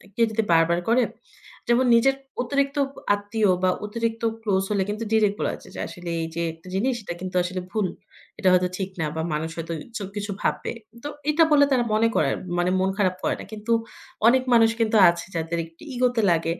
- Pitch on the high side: Yes, high, 205 Hz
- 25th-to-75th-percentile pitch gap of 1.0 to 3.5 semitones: No, average, 4.6 semitones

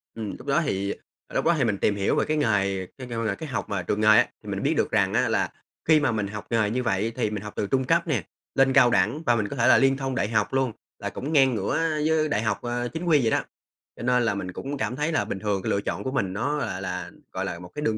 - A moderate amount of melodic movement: Yes, average, 5.0 semitones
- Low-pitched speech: Yes, low, 115 Hz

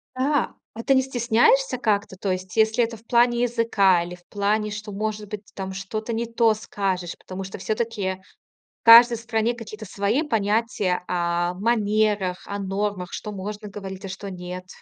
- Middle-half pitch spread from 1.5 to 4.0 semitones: Yes, average, 3.1 semitones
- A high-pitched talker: Yes, high, 210 Hz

